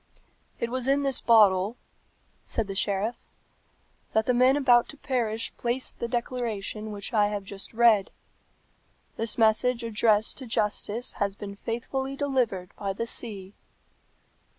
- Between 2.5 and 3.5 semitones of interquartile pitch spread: Yes, average, 3.2 semitones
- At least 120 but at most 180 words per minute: Yes, average, 140 wpm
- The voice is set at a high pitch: Yes, high, 230 Hz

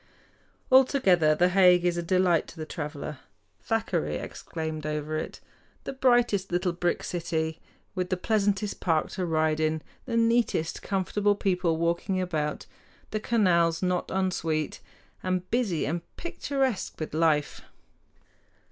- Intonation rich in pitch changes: No, average, 3.8 semitones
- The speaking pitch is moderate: Yes, medium, 180 Hz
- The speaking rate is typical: No, slow, 130 wpm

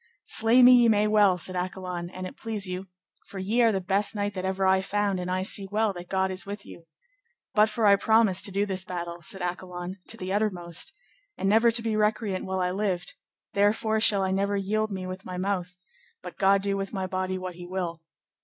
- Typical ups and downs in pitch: No, narrow, 2.2 semitones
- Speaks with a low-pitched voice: No, high, 190 Hz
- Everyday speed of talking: No, fast, 225 wpm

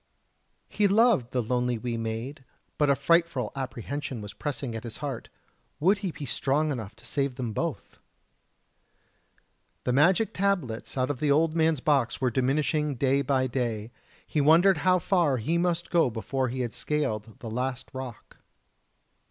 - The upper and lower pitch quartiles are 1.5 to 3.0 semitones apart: No, average, 4.3 semitones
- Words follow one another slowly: No, average, 165 wpm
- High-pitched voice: No, low, 135 Hz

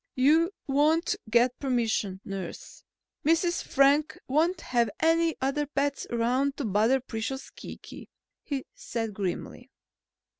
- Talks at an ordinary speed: No, slow, 115 wpm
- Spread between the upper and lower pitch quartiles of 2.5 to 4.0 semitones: No, average, 4.5 semitones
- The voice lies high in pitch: Yes, very high, 270 Hz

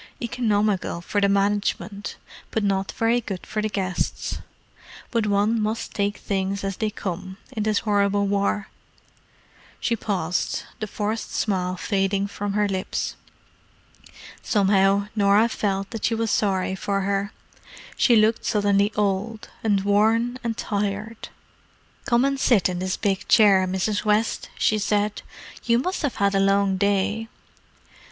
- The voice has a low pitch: No, high, 205 Hz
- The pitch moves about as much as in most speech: No, narrow, 1.7 semitones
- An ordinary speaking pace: Yes, average, 145 wpm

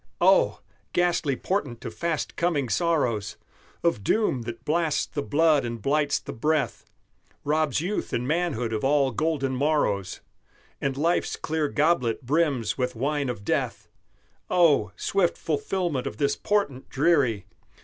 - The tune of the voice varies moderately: Yes, average, 4.8 semitones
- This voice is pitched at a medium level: Yes, medium, 145 Hz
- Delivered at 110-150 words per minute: Yes, average, 140 wpm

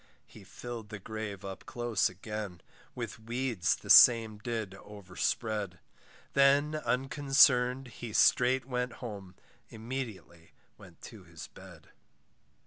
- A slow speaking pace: Yes, slow, 115 wpm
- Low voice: Yes, low, 115 Hz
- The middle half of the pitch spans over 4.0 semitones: No, average, 3.5 semitones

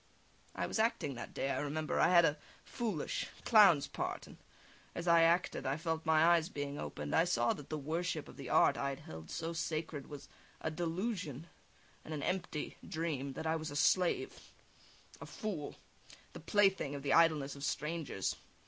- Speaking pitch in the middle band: Yes, medium, 155 Hz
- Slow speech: No, average, 185 wpm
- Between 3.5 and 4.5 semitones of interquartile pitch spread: No, average, 3.1 semitones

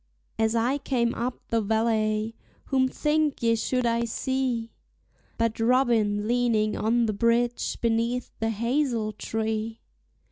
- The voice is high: Yes, high, 230 Hz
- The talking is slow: Yes, slow, 130 wpm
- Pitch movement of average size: No, narrow, 1.8 semitones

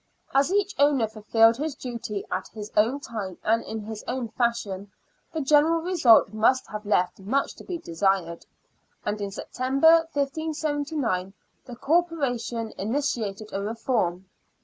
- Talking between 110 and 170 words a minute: Yes, average, 140 wpm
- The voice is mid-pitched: No, high, 235 Hz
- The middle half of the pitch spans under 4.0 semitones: No, wide, 5.5 semitones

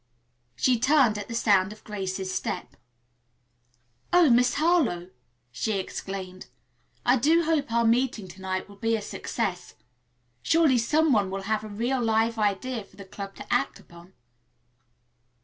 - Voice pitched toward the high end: Yes, high, 220 Hz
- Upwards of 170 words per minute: No, average, 150 wpm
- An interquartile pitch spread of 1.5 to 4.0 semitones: No, average, 4.6 semitones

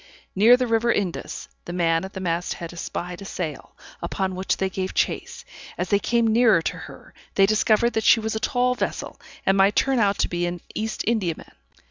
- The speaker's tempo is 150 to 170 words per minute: No, fast, 205 wpm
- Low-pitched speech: No, high, 195 Hz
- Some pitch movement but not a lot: Yes, average, 4.0 semitones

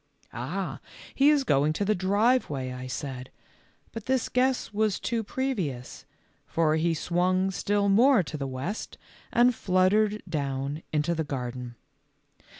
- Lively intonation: Yes, wide, 7.3 semitones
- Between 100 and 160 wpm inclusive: Yes, average, 140 wpm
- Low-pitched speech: No, medium, 180 Hz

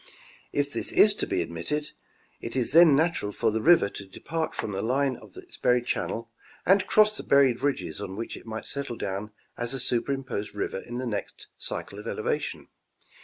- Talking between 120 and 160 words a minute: No, average, 185 wpm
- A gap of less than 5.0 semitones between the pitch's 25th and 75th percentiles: No, average, 5.3 semitones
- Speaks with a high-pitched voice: No, low, 125 Hz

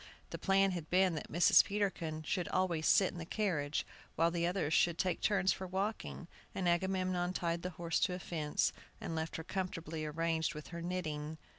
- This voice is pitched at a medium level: Yes, medium, 175 Hz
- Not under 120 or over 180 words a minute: No, average, 190 wpm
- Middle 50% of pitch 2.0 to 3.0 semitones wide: Yes, narrow, 2.5 semitones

